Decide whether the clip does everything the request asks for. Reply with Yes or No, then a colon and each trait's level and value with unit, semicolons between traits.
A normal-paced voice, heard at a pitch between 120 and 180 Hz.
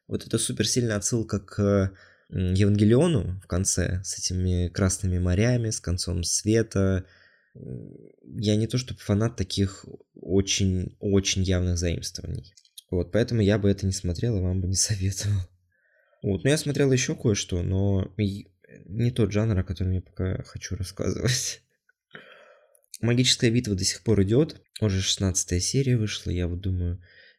No: average, 145 wpm; low, 100 Hz